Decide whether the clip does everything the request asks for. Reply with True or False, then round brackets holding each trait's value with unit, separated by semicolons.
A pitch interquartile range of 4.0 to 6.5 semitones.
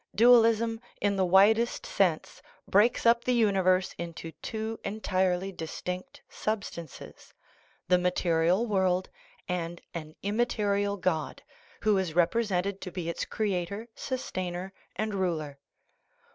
False (3.5 semitones)